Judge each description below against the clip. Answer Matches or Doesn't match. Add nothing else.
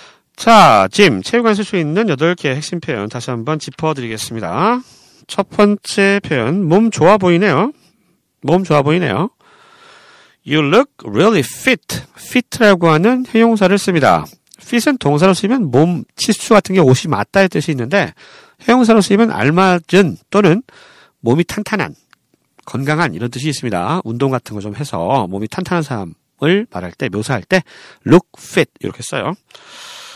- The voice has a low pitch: Doesn't match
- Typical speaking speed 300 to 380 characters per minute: Matches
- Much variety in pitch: Matches